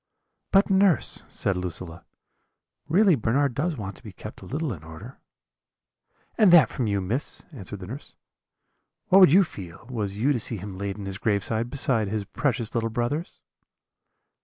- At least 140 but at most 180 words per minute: Yes, average, 170 wpm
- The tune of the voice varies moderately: No, wide, 6.7 semitones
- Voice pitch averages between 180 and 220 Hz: No, low, 115 Hz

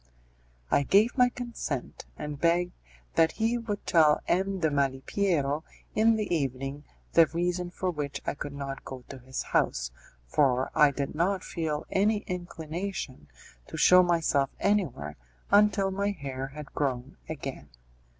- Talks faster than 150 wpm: No, average, 145 wpm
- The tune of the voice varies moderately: No, wide, 5.8 semitones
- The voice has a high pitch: No, medium, 160 Hz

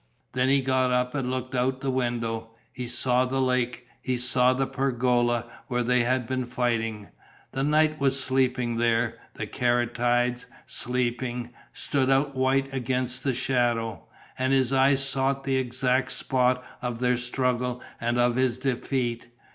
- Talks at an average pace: Yes, average, 155 wpm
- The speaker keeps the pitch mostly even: Yes, narrow, 1.4 semitones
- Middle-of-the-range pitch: No, low, 125 Hz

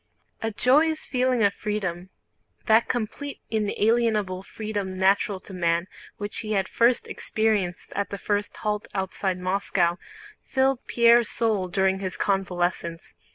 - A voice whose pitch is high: Yes, high, 205 Hz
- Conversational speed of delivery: No, slow, 120 wpm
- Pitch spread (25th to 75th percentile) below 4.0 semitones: Yes, average, 3.1 semitones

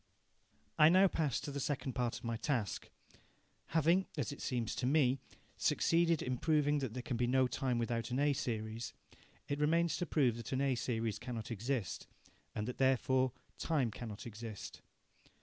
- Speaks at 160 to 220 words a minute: Yes, average, 175 wpm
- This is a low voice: Yes, low, 130 Hz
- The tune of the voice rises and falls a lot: No, average, 3.9 semitones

